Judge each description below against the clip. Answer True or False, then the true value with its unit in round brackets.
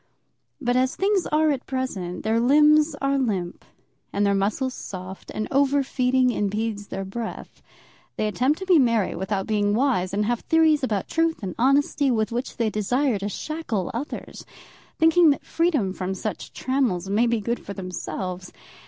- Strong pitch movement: True (5.7 semitones)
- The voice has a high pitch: True (235 Hz)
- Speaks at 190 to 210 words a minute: False (170 wpm)